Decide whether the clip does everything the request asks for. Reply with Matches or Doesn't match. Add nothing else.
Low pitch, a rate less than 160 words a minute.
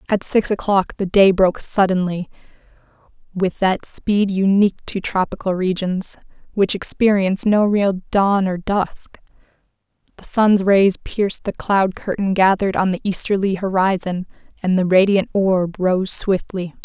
Doesn't match